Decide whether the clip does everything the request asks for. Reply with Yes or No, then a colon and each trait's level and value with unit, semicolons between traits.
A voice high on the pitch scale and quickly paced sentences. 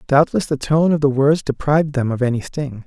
No: medium, 140 Hz; fast, 230 wpm